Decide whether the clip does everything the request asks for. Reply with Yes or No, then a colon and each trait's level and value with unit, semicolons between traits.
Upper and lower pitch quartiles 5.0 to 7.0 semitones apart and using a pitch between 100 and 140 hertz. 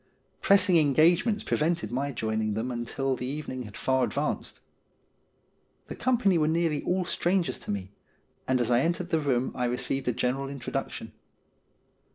Yes: wide, 5.4 semitones; low, 135 Hz